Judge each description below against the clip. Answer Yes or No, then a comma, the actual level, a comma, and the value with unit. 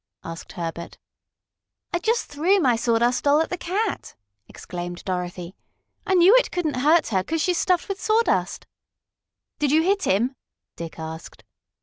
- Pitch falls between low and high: No, very high, 290 Hz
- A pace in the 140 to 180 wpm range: Yes, average, 150 wpm